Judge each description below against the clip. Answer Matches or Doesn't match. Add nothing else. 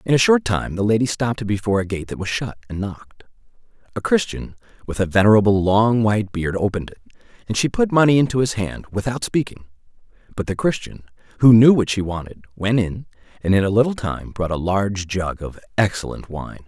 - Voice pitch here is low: Matches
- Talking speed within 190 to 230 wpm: Matches